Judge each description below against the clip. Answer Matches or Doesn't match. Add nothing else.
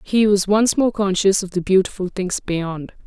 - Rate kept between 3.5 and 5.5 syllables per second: Matches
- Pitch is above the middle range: Matches